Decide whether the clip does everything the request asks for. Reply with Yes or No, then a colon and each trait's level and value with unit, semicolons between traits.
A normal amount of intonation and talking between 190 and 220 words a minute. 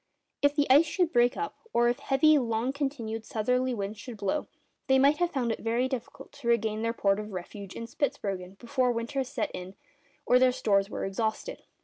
Yes: average, 3.8 semitones; fast, 205 wpm